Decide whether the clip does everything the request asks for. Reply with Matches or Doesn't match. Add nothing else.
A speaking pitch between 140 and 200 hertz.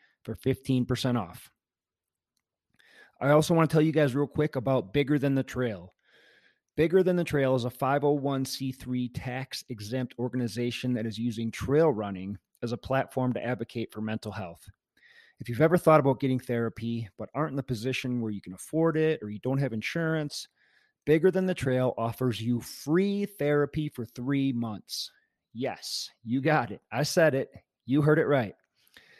Doesn't match